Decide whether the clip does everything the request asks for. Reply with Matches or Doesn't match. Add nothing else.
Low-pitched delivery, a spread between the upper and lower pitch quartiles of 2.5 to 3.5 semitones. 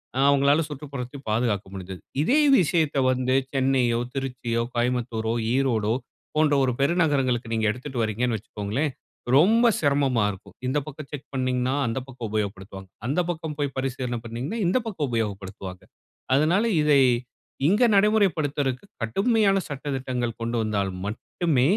Doesn't match